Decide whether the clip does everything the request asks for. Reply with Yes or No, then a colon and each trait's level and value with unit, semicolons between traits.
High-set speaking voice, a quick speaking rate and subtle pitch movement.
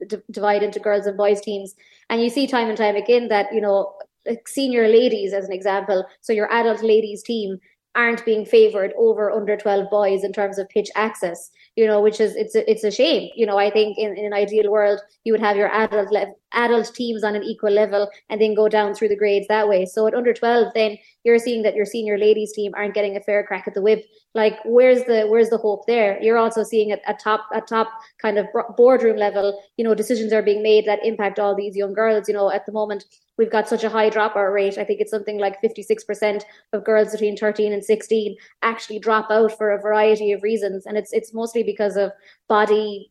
Yes: high, 215 Hz; fast, 235 wpm; narrow, 1.4 semitones